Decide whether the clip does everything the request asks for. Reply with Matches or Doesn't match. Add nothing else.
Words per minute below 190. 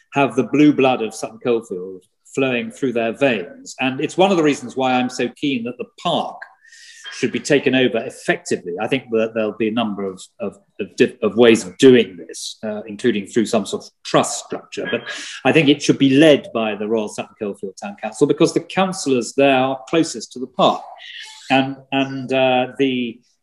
Doesn't match